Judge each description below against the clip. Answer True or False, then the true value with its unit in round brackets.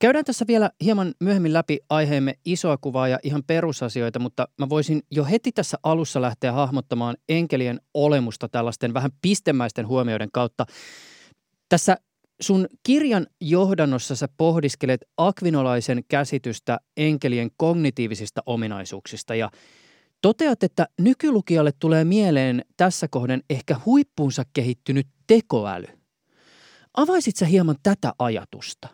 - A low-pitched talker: False (145 Hz)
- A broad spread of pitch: True (6.0 semitones)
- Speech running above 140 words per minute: False (115 wpm)